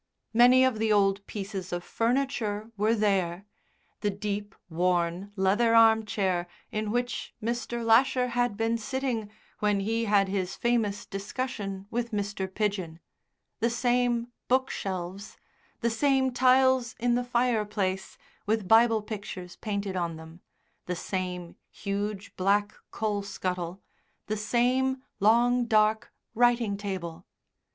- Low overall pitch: No, high, 210 Hz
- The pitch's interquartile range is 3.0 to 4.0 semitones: Yes, average, 3.5 semitones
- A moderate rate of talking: No, slow, 125 wpm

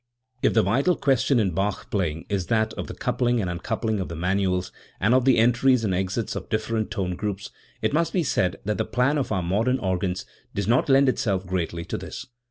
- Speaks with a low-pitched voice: Yes, low, 105 Hz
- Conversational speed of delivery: No, fast, 215 wpm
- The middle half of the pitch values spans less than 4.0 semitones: No, average, 4.7 semitones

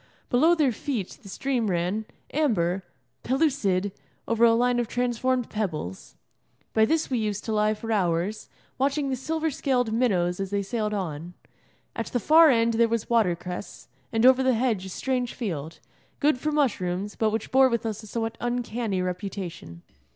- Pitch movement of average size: Yes, average, 4.7 semitones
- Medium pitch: No, high, 225 Hz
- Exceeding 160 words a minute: Yes, average, 170 wpm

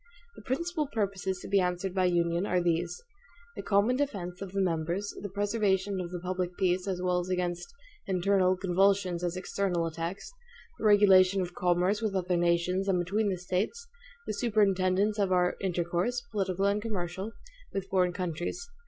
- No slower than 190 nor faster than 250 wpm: No, average, 165 wpm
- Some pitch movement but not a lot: No, narrow, 2.1 semitones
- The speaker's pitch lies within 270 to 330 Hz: No, medium, 185 Hz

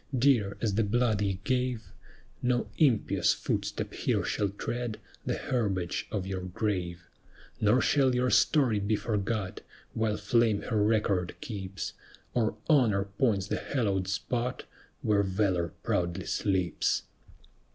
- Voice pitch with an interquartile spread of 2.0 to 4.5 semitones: Yes, average, 3.6 semitones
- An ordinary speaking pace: No, slow, 130 wpm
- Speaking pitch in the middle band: No, low, 105 Hz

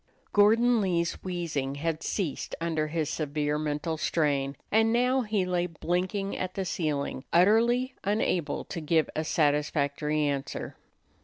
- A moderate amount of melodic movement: Yes, average, 4.8 semitones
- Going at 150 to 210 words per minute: No, slow, 135 wpm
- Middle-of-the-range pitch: Yes, medium, 165 Hz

